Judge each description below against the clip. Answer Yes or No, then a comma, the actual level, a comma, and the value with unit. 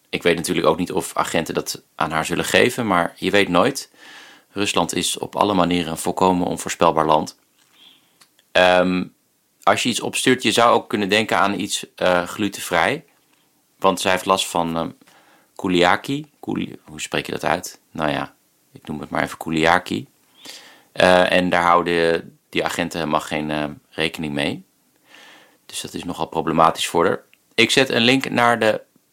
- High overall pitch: No, very low, 90 Hz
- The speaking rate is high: No, average, 175 wpm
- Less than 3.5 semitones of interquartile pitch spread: Yes, average, 2.8 semitones